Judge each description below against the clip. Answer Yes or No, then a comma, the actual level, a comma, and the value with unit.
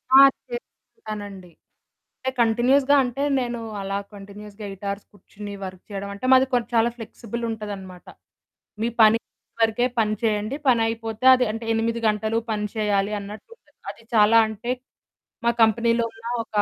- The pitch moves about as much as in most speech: No, narrow, 2.3 semitones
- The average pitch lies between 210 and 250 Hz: Yes, high, 220 Hz